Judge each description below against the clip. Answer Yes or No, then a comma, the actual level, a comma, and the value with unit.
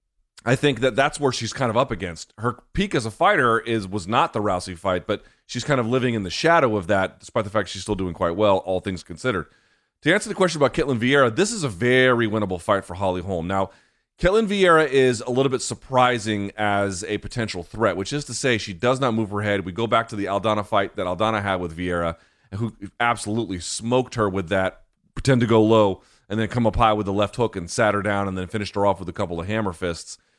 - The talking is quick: Yes, fast, 250 wpm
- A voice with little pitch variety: No, average, 4.3 semitones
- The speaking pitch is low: Yes, low, 110 Hz